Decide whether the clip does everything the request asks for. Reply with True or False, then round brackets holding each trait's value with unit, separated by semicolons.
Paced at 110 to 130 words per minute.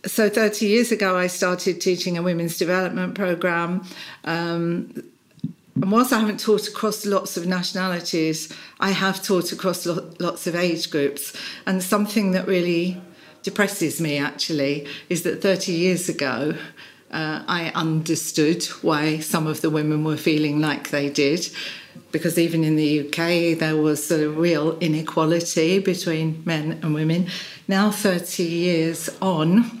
False (150 wpm)